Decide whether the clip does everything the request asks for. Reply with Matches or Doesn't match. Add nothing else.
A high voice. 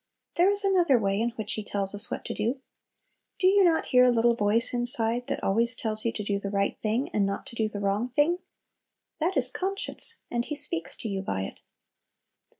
Matches